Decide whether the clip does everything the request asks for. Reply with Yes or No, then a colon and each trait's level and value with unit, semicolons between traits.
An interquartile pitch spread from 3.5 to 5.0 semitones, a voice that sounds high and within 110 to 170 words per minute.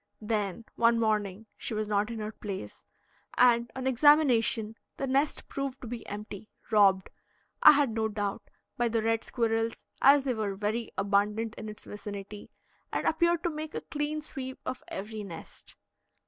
Yes: average, 3.8 semitones; high, 225 Hz; average, 165 wpm